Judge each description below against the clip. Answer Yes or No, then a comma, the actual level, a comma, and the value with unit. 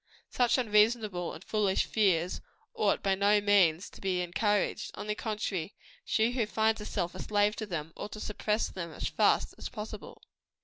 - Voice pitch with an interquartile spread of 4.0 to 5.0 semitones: No, average, 2.8 semitones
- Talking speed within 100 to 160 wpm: No, average, 175 wpm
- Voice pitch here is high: Yes, high, 205 Hz